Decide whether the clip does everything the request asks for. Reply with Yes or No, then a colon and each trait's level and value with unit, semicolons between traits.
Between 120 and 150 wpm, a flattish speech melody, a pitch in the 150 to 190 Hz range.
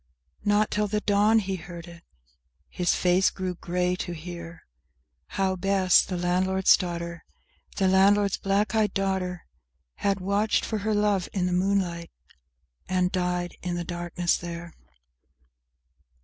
Yes: slow, 135 wpm; narrow, 2.1 semitones; medium, 185 Hz